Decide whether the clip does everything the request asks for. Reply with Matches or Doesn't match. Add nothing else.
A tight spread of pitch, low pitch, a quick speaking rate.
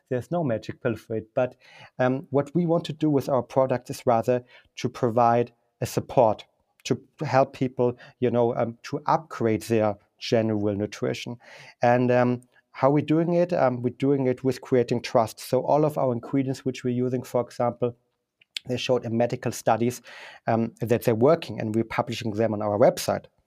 Doesn't match